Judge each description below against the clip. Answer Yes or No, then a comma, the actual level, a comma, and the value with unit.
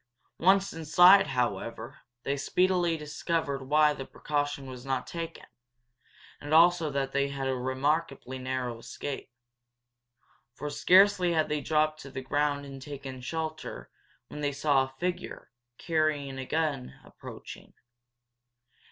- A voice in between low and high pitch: Yes, medium, 145 Hz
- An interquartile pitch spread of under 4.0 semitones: Yes, average, 3.3 semitones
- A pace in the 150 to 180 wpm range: No, slow, 135 wpm